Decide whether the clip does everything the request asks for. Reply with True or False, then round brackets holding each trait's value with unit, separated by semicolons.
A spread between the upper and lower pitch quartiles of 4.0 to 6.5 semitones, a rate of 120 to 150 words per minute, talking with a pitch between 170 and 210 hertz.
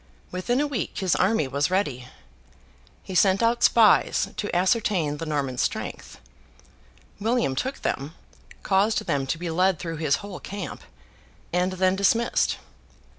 True (4.9 semitones; 140 wpm; 185 Hz)